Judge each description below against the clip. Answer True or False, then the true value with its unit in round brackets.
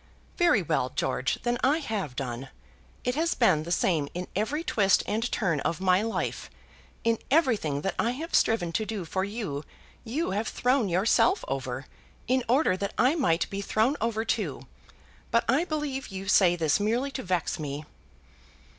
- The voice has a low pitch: False (215 Hz)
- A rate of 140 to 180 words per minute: True (175 wpm)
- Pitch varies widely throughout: True (6.4 semitones)